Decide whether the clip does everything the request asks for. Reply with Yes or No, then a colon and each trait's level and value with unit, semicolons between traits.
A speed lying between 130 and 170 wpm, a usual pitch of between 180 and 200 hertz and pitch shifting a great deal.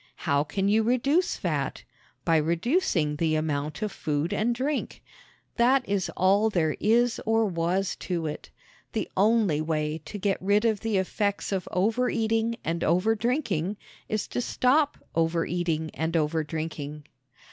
Yes: average, 140 wpm; high, 190 Hz; wide, 5.8 semitones